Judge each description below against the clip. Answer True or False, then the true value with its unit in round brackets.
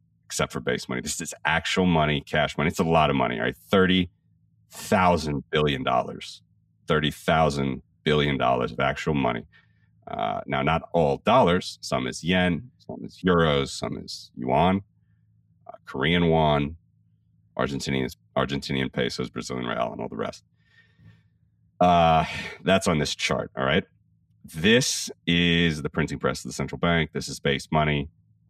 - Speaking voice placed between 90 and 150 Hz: False (80 Hz)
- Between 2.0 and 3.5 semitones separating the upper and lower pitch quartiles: False (4.3 semitones)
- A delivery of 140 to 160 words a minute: True (155 wpm)